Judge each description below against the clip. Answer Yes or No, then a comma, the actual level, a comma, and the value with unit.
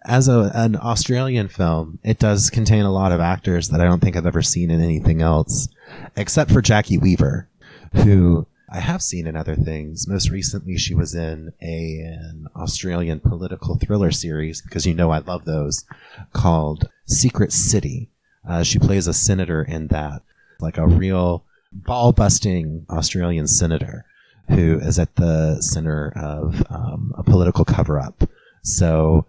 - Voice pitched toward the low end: Yes, very low, 85 Hz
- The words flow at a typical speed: Yes, average, 160 wpm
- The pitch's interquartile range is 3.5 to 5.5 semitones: Yes, average, 4.3 semitones